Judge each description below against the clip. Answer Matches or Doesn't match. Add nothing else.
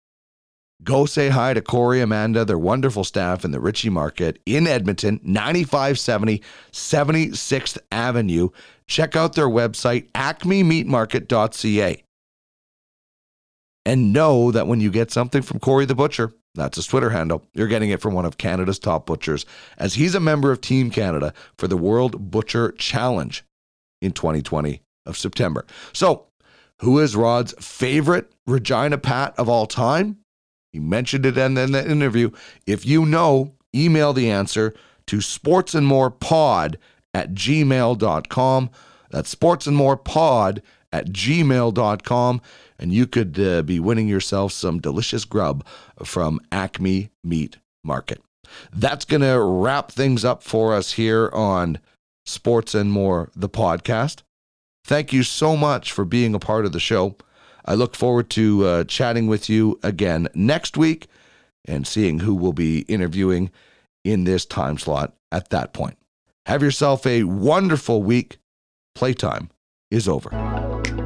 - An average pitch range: Doesn't match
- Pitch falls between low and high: Doesn't match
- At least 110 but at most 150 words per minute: Matches